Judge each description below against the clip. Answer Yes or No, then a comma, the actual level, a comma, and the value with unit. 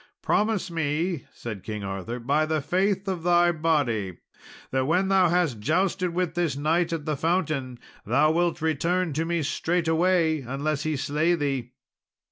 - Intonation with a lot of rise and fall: No, average, 4.0 semitones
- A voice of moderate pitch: Yes, medium, 160 Hz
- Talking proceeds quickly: No, average, 155 wpm